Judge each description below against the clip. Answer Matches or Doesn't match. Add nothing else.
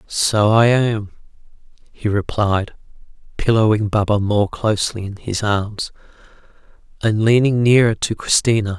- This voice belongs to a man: Matches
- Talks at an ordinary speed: Doesn't match